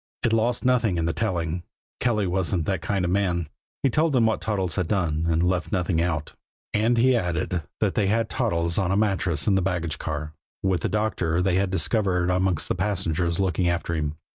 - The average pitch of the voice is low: Yes, very low, 90 Hz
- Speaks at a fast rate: Yes, fast, 210 wpm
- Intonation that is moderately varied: Yes, average, 3.7 semitones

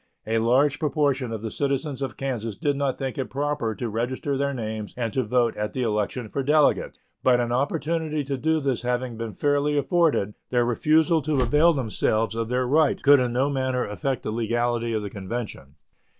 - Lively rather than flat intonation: No, average, 3.9 semitones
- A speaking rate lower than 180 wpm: No, average, 195 wpm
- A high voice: No, low, 130 Hz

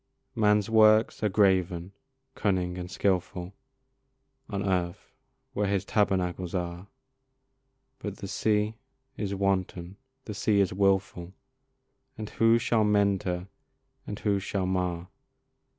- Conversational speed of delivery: No, slow, 120 wpm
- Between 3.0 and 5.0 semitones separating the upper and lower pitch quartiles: No, narrow, 2.4 semitones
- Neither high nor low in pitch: No, low, 100 Hz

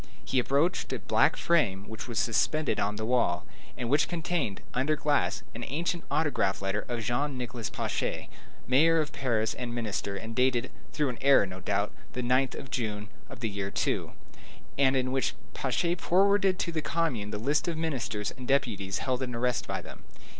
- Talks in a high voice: No, low, 125 Hz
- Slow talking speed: No, average, 185 wpm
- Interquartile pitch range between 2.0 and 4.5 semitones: No, average, 5.2 semitones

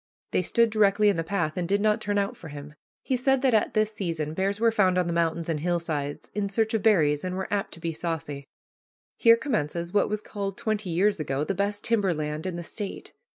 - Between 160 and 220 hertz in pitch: Yes, high, 190 Hz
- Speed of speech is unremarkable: No, fast, 235 wpm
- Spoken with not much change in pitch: No, average, 4.4 semitones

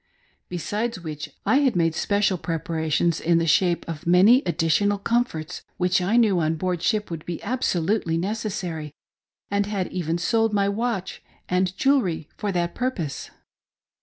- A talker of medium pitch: Yes, medium, 180 Hz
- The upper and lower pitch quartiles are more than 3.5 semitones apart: Yes, average, 4.0 semitones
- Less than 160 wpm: Yes, average, 150 wpm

